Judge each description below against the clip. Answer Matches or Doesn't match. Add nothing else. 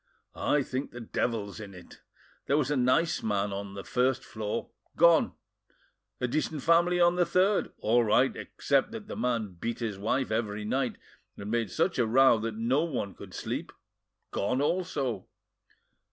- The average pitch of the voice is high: Doesn't match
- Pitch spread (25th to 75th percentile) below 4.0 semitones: Doesn't match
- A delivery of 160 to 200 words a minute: Matches